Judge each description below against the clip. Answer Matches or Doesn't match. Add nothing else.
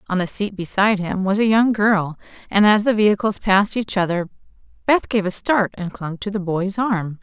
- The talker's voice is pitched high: Matches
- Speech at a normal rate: Doesn't match